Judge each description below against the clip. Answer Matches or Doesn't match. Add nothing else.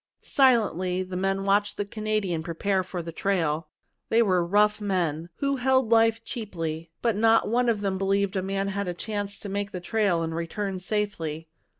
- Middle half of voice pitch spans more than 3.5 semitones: Doesn't match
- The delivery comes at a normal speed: Matches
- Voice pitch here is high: Matches